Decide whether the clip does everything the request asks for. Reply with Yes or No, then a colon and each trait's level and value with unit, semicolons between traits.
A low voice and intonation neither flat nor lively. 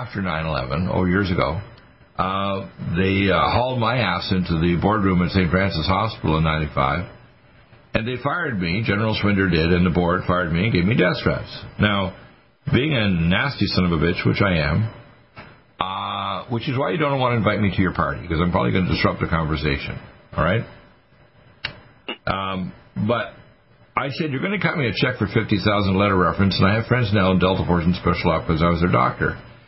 Yes: very low, 95 Hz; average, 4.7 semitones